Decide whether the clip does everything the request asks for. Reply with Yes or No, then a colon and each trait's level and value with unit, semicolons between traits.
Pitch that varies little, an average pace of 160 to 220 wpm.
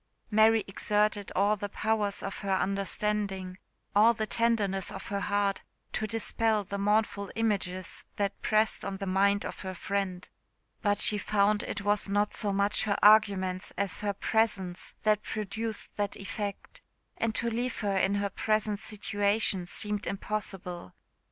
No: narrow, 1.4 semitones; average, 150 wpm